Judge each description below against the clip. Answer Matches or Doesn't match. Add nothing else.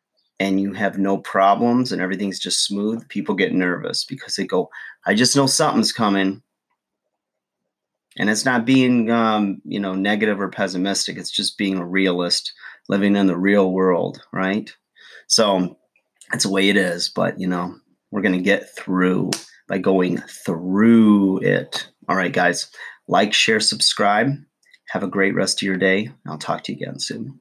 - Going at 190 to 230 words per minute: Doesn't match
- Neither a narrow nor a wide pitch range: Doesn't match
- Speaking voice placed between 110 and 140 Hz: Doesn't match